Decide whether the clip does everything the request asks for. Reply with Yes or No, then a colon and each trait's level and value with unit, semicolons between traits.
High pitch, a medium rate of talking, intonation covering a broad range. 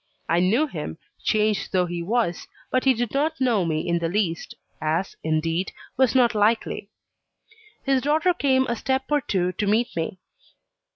Yes: high, 210 Hz; average, 170 wpm; wide, 7.1 semitones